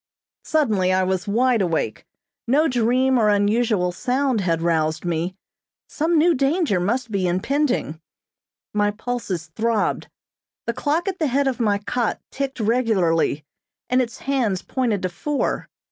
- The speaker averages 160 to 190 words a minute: No, average, 145 wpm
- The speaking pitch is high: Yes, high, 225 Hz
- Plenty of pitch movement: Yes, wide, 6.0 semitones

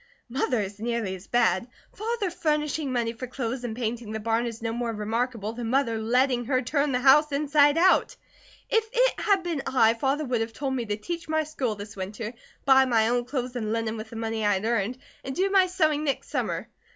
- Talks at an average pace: No, fast, 215 wpm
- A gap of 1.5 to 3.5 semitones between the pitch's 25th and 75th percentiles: No, average, 4.3 semitones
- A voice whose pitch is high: Yes, high, 245 Hz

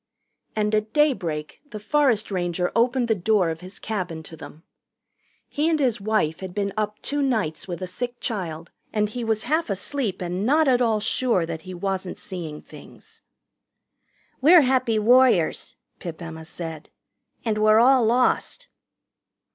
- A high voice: Yes, high, 210 Hz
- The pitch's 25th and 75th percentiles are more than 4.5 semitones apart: Yes, wide, 5.6 semitones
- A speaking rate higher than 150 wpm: Yes, average, 160 wpm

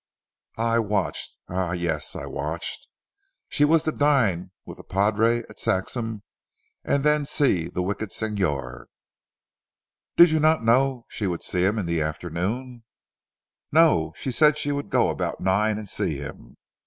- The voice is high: No, low, 110 Hz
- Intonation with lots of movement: Yes, wide, 7.2 semitones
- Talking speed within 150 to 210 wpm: Yes, average, 155 wpm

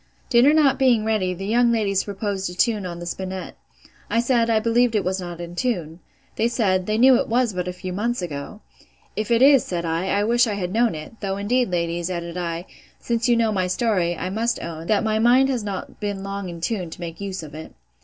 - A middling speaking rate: No, fast, 235 wpm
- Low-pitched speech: No, high, 200 Hz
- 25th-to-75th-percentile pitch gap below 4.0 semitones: No, average, 4.5 semitones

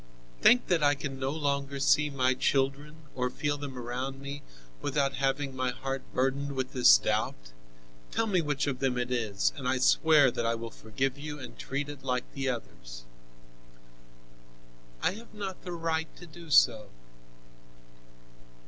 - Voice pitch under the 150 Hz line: Yes, low, 135 Hz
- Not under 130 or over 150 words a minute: No, average, 165 wpm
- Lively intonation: No, narrow, 2.4 semitones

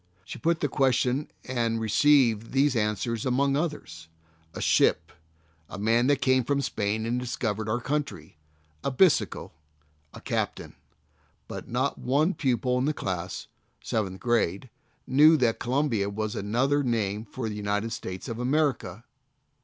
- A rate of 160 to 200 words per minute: No, average, 145 wpm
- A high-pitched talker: No, low, 120 Hz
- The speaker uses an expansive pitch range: No, average, 4.4 semitones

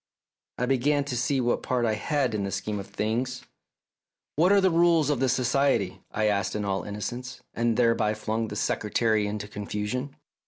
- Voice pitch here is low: Yes, low, 120 Hz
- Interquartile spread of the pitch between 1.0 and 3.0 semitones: No, average, 4.0 semitones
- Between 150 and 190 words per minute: Yes, average, 185 wpm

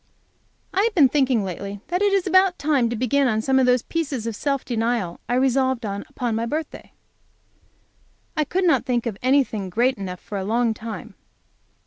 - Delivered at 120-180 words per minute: No, average, 190 wpm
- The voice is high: Yes, very high, 250 Hz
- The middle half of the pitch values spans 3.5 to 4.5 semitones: Yes, average, 4.2 semitones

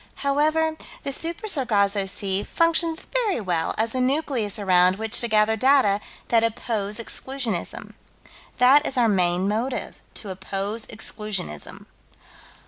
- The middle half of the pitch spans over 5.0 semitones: Yes, wide, 5.4 semitones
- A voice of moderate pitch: No, high, 225 Hz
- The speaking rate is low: Yes, slow, 130 wpm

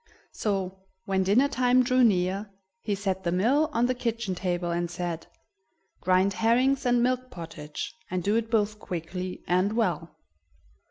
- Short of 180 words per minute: Yes, average, 155 wpm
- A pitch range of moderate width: Yes, average, 4.8 semitones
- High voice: Yes, high, 200 Hz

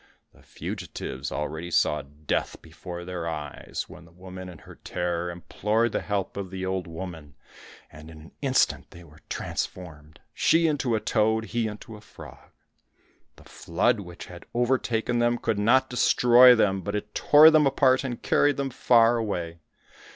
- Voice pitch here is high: No, very low, 95 Hz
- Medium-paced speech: Yes, average, 165 wpm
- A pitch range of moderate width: No, wide, 5.9 semitones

